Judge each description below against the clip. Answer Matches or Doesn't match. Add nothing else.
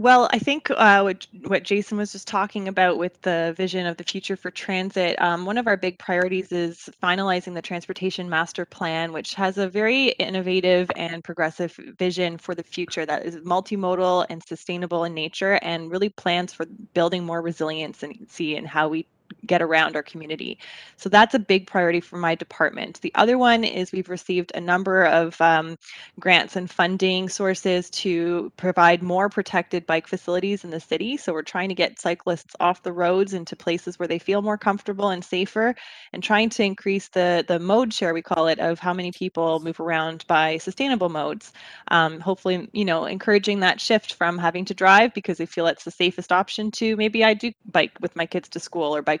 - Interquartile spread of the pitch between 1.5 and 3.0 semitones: Matches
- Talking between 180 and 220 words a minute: Matches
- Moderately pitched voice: Matches